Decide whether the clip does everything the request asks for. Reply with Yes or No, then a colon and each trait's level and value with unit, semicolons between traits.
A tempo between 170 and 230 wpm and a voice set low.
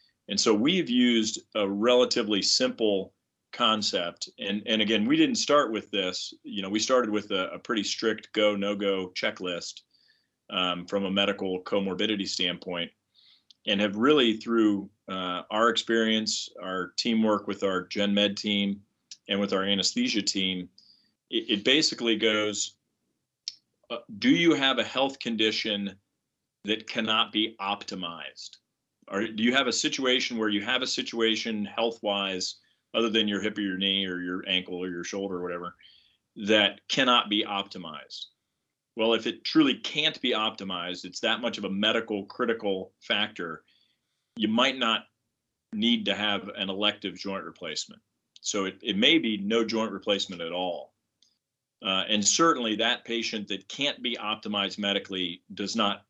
No: average, 155 wpm; low, 105 Hz